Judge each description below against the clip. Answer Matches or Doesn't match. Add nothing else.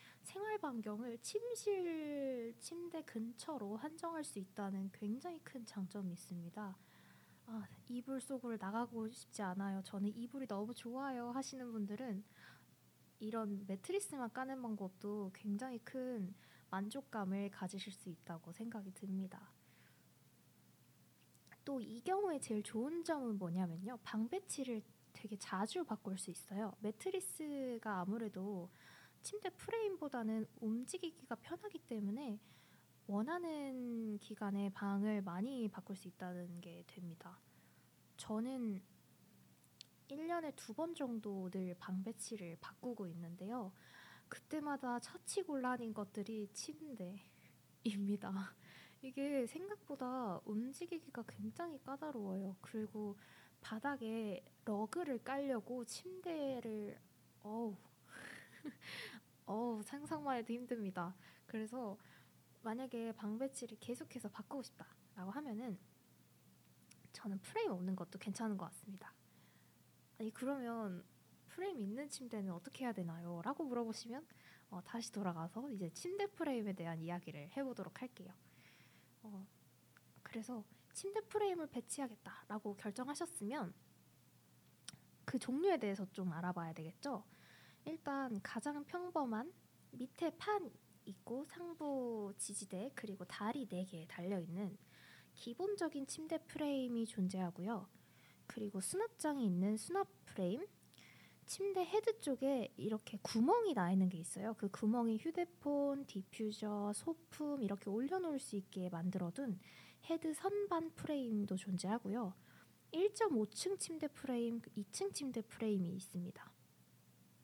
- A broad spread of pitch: Matches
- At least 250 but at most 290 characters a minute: Matches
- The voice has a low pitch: Doesn't match